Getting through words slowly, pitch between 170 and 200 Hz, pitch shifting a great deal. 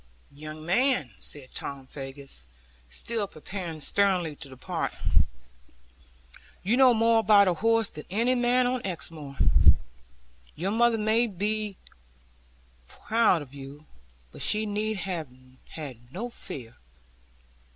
Yes: slow, 120 wpm; high, 190 Hz; wide, 7.2 semitones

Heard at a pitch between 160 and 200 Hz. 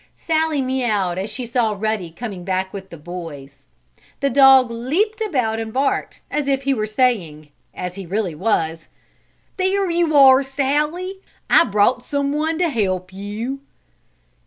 No: high, 240 Hz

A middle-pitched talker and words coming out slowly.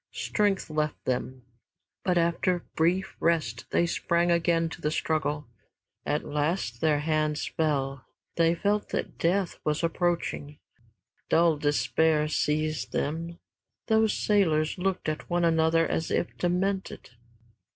Yes: medium, 165 Hz; slow, 125 wpm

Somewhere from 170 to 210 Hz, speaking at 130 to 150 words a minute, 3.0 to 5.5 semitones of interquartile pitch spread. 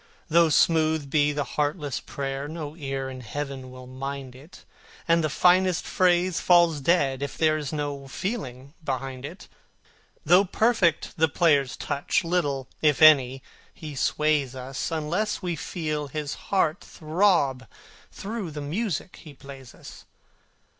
No: medium, 150 Hz; average, 140 wpm; average, 3.8 semitones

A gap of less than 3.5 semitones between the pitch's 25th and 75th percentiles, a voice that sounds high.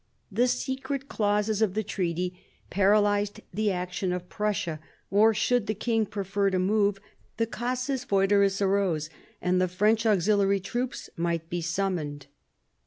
Yes: average, 3.0 semitones; high, 200 Hz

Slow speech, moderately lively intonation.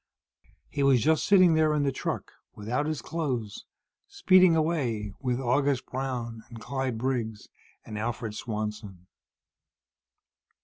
Yes: slow, 125 wpm; average, 5.0 semitones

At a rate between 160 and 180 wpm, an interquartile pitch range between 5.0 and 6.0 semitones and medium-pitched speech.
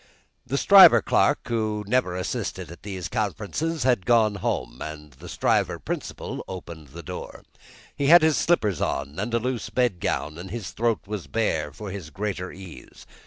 No: average, 170 wpm; average, 5.3 semitones; low, 105 Hz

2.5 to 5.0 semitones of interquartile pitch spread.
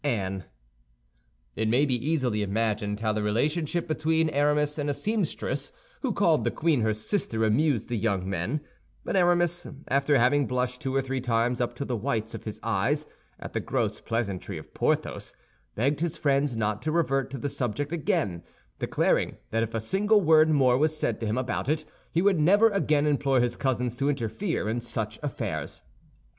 No: wide, 5.4 semitones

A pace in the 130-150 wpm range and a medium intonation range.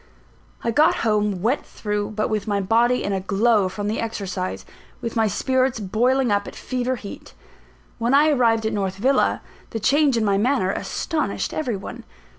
No: average, 180 wpm; average, 3.7 semitones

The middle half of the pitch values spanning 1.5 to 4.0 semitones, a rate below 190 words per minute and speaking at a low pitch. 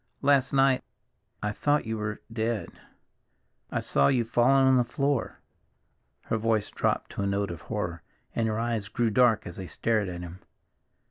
Yes: average, 3.5 semitones; average, 170 wpm; low, 115 Hz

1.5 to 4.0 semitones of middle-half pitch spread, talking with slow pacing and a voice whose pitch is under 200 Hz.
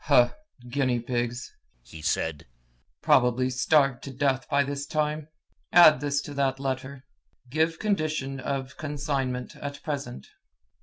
Yes: narrow, 2.4 semitones; slow, 125 wpm; low, 135 Hz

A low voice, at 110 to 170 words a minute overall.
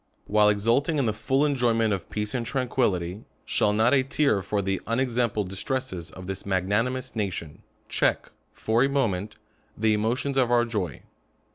Yes: low, 110 Hz; average, 165 wpm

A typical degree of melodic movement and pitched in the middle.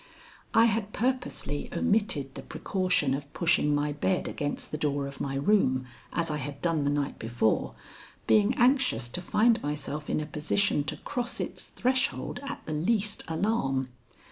No: wide, 6.9 semitones; medium, 155 Hz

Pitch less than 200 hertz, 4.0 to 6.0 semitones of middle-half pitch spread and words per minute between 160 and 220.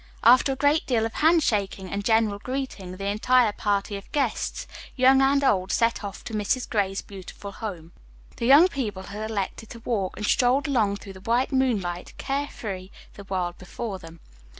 No: high, 215 Hz; average, 4.5 semitones; average, 180 wpm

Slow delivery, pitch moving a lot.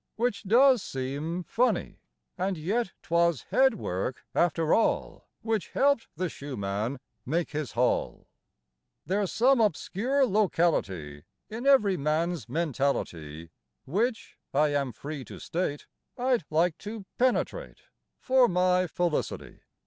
Yes: slow, 120 wpm; wide, 7.5 semitones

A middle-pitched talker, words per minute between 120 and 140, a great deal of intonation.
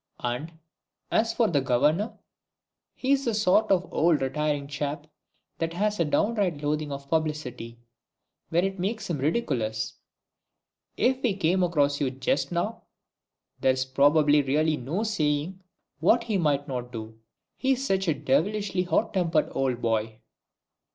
Yes: medium, 155 Hz; slow, 135 wpm; wide, 5.7 semitones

